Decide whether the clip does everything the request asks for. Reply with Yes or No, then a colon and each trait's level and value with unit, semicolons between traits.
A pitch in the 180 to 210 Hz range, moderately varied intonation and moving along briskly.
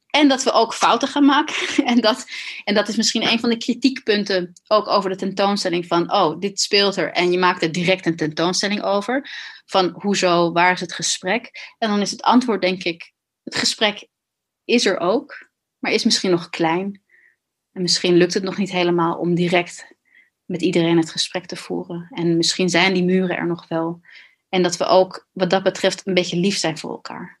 Yes: medium, 185 Hz; average, 3.5 semitones; fast, 205 wpm